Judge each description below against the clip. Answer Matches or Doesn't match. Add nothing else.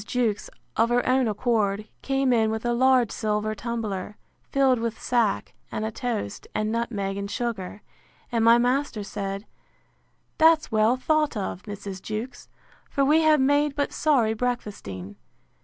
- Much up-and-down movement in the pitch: Doesn't match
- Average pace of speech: Matches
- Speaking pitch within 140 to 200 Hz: Doesn't match